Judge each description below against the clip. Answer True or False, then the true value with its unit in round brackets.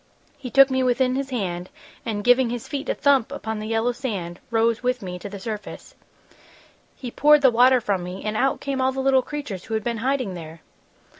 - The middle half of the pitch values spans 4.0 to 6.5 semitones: True (4.3 semitones)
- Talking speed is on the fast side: True (215 wpm)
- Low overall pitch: False (240 Hz)